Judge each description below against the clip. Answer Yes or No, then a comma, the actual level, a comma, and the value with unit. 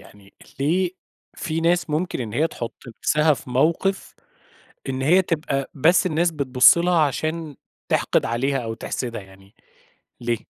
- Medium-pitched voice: Yes, medium, 150 Hz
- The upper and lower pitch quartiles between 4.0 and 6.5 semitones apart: Yes, average, 5.2 semitones